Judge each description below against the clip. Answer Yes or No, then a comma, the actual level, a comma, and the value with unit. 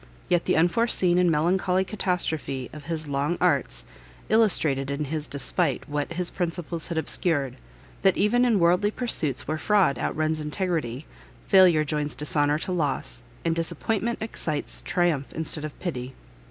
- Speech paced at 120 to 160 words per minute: Yes, average, 150 wpm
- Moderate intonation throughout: Yes, average, 3.6 semitones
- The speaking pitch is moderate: Yes, medium, 160 Hz